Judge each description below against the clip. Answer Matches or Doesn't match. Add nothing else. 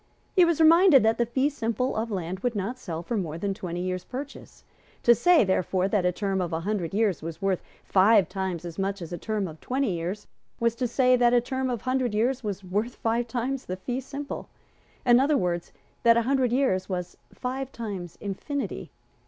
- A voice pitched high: Matches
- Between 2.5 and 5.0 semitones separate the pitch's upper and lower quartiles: Doesn't match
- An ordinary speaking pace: Doesn't match